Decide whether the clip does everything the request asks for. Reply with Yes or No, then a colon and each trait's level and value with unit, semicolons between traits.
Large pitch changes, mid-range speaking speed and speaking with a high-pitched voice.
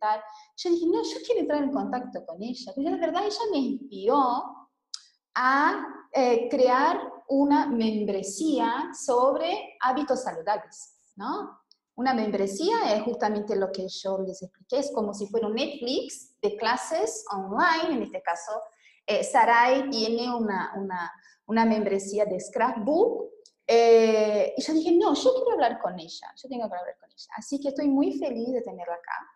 Yes: wide, 5.8 semitones; average, 160 wpm; high, 245 Hz